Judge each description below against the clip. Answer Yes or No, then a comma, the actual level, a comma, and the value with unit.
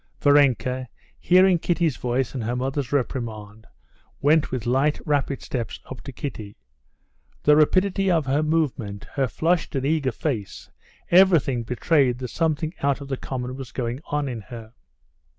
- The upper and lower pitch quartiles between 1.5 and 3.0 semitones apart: No, average, 3.9 semitones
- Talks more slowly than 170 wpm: Yes, average, 150 wpm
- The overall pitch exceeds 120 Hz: Yes, low, 135 Hz